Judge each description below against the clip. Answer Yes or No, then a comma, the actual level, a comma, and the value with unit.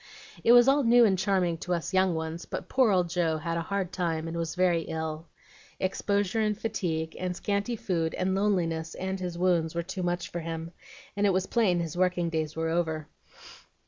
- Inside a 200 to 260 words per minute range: Yes, fast, 205 wpm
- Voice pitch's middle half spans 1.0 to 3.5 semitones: Yes, average, 2.8 semitones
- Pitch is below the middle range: No, medium, 175 Hz